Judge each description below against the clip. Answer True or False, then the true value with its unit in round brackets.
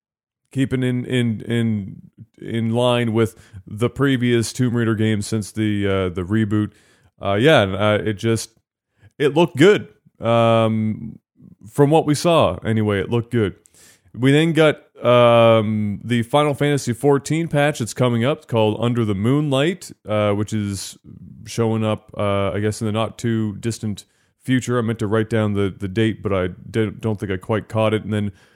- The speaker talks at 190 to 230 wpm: False (175 wpm)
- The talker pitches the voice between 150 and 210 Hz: False (110 Hz)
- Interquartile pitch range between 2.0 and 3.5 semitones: True (2.7 semitones)